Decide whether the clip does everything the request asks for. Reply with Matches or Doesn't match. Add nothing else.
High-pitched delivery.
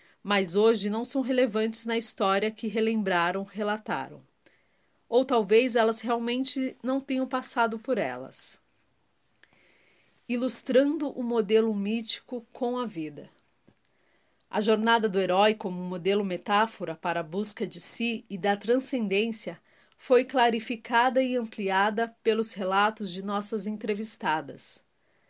Matches